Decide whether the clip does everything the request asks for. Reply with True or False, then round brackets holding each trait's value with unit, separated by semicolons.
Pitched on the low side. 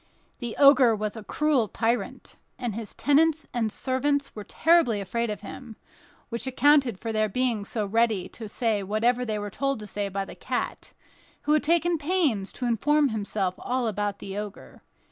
False (235 Hz)